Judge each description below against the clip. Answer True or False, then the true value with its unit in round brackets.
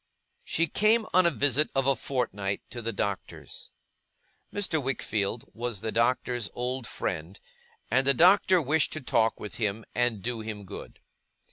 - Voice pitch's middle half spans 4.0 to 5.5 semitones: True (4.8 semitones)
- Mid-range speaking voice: False (120 Hz)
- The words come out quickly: False (155 wpm)